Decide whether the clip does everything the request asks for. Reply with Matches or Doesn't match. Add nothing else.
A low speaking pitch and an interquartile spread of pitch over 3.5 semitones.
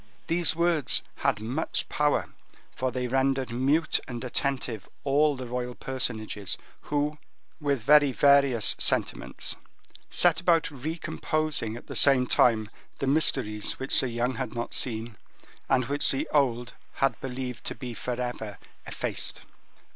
Doesn't match